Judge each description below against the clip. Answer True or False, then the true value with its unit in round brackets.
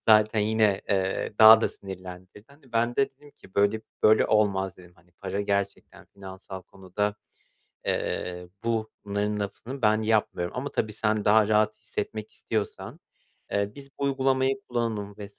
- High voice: False (105 Hz)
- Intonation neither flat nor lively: False (2.1 semitones)